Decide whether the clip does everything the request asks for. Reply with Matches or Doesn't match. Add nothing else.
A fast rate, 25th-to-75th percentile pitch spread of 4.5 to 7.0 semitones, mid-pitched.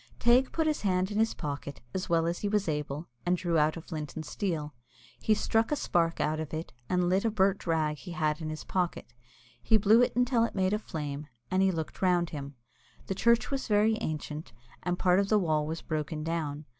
Matches